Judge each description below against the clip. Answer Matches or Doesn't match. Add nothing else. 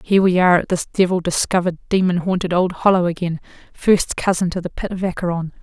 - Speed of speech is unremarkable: Matches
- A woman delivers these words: Matches